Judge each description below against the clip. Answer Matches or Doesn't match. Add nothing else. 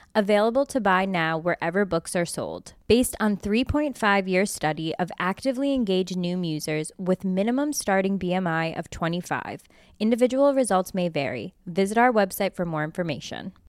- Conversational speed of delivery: Matches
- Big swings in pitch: Doesn't match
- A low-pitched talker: Doesn't match